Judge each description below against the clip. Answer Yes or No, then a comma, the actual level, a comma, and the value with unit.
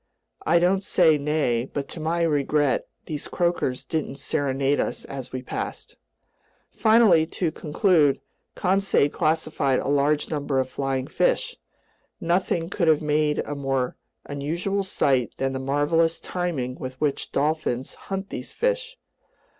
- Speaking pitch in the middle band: Yes, medium, 150 Hz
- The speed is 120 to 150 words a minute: Yes, average, 140 wpm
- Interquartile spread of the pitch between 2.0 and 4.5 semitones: Yes, average, 3.9 semitones